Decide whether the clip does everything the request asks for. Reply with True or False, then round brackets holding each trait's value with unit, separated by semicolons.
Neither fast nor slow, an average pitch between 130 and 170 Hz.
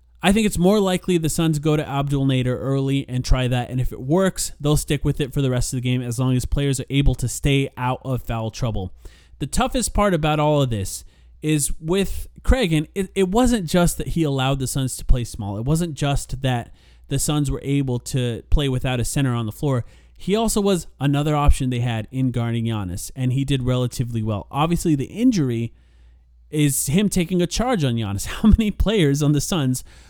False (220 wpm; 135 Hz)